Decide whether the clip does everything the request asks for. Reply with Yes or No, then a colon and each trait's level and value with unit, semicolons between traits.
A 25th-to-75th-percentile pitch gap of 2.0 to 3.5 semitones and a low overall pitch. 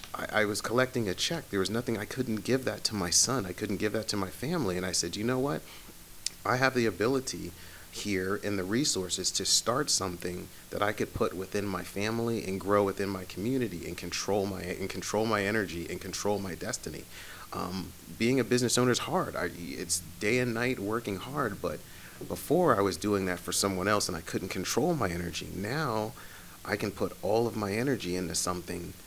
No: average, 3.9 semitones; low, 100 Hz